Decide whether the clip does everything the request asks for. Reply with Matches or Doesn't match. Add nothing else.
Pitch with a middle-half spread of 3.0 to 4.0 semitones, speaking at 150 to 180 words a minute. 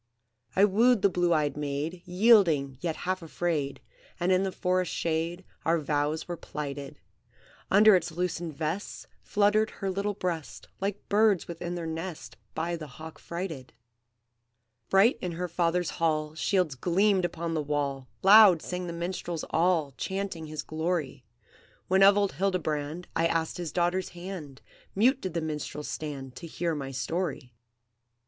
Matches